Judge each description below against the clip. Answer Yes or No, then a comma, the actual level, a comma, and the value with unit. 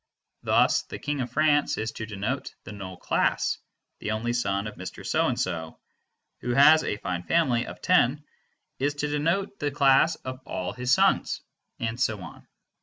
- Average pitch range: No, wide, 5.8 semitones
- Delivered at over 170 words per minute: Yes, average, 180 wpm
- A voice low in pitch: Yes, low, 125 Hz